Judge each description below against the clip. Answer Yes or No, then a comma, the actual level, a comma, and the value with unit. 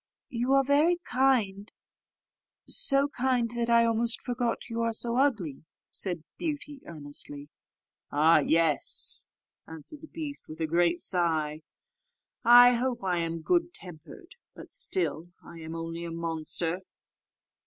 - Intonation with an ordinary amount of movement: No, wide, 8.0 semitones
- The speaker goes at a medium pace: No, slow, 130 wpm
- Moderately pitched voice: No, high, 225 Hz